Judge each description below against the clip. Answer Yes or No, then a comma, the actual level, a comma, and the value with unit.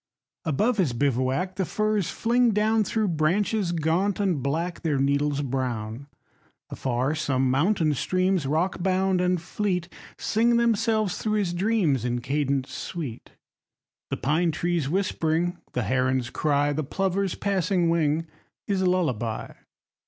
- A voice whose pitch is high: No, medium, 170 Hz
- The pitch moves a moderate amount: No, wide, 5.7 semitones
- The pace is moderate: No, slow, 130 wpm